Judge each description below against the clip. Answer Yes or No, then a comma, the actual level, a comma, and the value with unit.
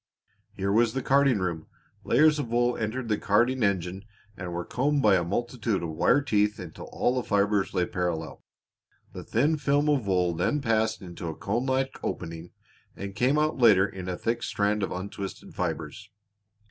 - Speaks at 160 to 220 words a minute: Yes, average, 180 wpm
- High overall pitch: No, low, 105 Hz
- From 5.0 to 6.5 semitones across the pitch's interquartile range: Yes, wide, 5.5 semitones